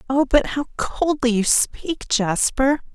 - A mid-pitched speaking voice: No, very high, 260 Hz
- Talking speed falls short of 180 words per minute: Yes, average, 140 wpm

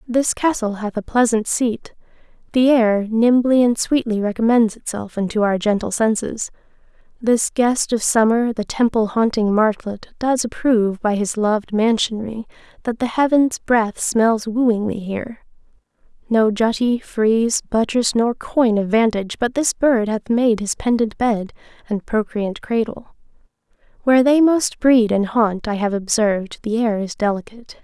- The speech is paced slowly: No, average, 150 wpm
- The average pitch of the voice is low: No, high, 225 Hz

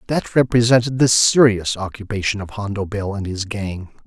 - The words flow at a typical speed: Yes, average, 160 wpm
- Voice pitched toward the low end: Yes, low, 105 Hz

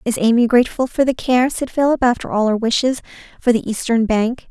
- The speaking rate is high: Yes, fast, 215 wpm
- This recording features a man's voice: No, female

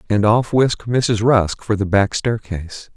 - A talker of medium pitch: No, low, 110 Hz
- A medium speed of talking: Yes, average, 180 wpm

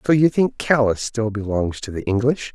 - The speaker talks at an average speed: No, fast, 215 wpm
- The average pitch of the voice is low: Yes, low, 120 Hz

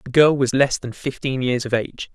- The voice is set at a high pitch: No, low, 130 Hz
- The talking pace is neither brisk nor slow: No, fast, 250 wpm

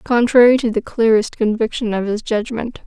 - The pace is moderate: Yes, average, 170 wpm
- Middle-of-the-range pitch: No, high, 225 Hz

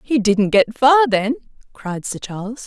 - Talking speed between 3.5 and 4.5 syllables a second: Yes, 4.1 syllables/s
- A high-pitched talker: Yes, high, 230 Hz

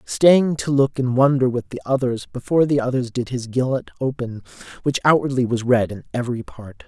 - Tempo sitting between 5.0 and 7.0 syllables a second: Yes, 5.4 syllables/s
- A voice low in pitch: Yes, low, 125 Hz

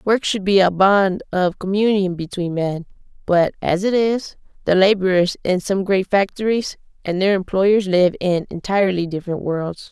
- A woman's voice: Yes, female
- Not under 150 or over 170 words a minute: Yes, average, 165 wpm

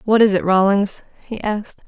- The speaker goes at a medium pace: Yes, average, 190 wpm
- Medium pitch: No, high, 205 Hz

